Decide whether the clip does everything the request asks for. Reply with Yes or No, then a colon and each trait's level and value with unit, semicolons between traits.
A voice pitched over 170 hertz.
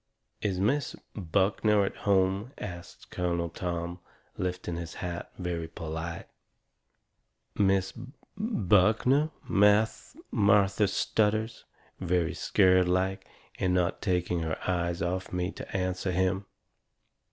No: very low, 95 Hz